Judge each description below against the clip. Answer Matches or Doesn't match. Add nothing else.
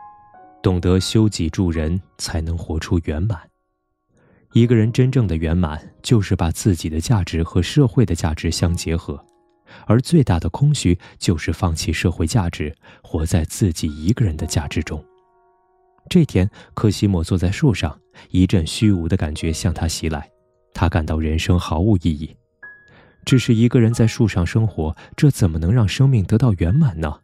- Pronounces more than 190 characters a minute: Matches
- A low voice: Matches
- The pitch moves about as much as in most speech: Doesn't match